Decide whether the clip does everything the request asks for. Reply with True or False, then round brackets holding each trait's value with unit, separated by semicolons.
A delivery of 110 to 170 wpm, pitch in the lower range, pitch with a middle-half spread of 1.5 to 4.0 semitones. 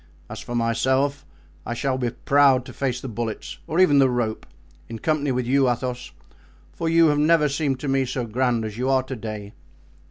False (200 wpm; 130 Hz; 2.9 semitones)